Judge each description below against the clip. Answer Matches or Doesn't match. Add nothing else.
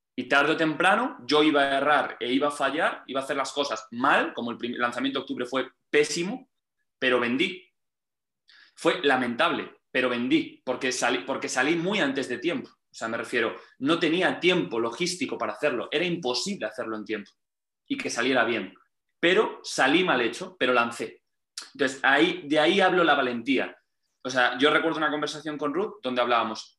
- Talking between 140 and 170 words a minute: Doesn't match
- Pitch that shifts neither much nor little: Doesn't match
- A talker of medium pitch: Matches